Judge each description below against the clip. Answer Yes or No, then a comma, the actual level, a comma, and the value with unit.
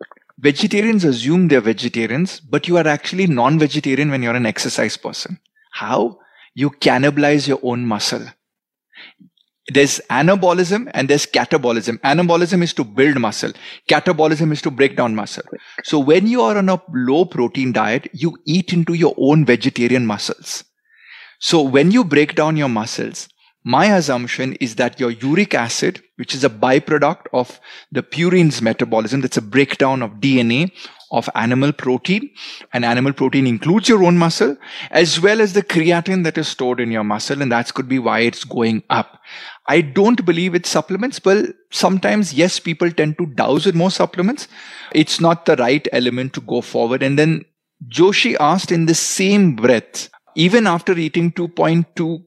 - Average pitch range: No, wide, 5.7 semitones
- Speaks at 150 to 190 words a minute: Yes, average, 165 wpm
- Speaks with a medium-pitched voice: Yes, medium, 155 Hz